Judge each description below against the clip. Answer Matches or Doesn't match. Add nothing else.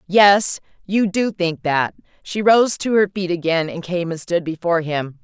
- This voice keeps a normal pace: Matches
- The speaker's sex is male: Doesn't match